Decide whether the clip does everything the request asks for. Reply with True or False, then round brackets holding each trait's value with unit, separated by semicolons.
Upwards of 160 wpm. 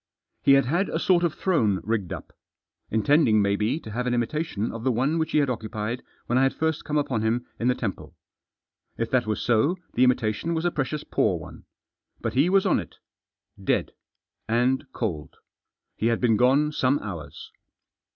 True (190 wpm)